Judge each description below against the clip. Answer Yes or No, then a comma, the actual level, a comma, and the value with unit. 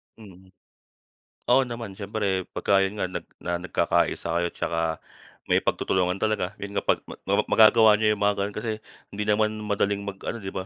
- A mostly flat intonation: Yes, narrow, 2.3 semitones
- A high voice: No, low, 100 Hz